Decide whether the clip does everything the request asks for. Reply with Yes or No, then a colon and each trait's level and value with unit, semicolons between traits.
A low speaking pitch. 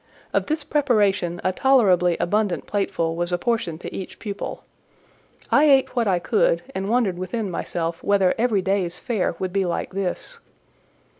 No: high, 195 Hz